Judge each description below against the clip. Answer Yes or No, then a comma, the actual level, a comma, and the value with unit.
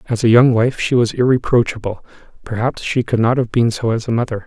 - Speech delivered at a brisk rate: Yes, fast, 230 wpm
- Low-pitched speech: Yes, low, 120 Hz